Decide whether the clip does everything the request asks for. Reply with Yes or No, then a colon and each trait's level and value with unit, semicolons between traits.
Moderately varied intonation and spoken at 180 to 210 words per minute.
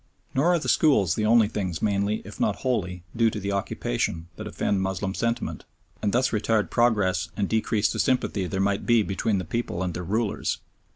Yes: average, 3.2 semitones; average, 195 wpm